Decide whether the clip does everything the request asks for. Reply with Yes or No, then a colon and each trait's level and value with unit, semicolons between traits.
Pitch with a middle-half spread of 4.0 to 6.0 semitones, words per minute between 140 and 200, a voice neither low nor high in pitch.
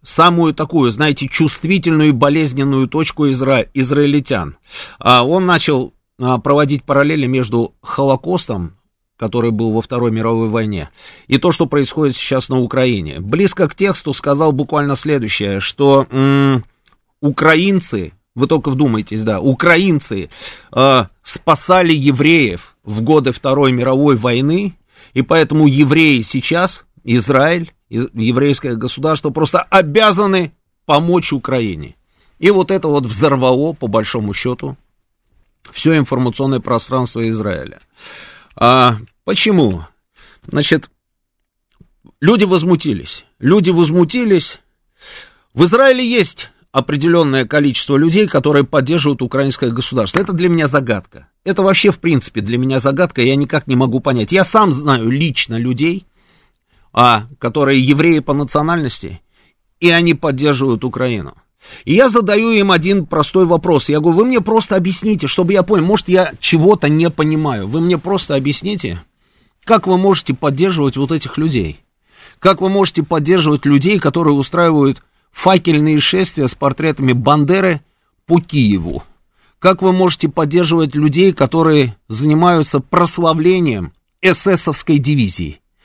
No: average, 5.1 semitones; average, 120 wpm; medium, 145 Hz